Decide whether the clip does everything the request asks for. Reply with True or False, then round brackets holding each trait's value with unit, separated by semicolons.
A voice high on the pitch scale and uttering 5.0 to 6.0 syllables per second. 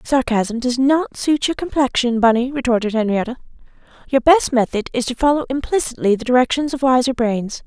True (255 Hz; 5.5 syllables/s)